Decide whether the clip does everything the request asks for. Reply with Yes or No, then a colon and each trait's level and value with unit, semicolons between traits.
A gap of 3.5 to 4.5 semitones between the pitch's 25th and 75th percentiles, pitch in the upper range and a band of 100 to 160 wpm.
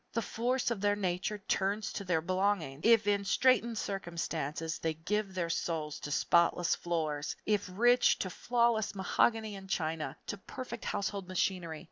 Yes: average, 4.1 semitones; high, 195 Hz; average, 155 wpm